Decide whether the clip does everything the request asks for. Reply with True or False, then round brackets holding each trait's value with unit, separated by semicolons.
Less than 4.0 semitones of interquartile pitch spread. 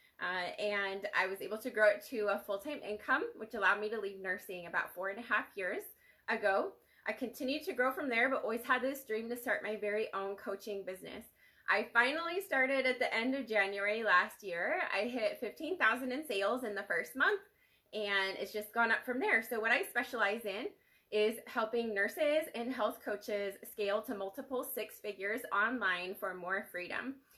False (4.5 semitones)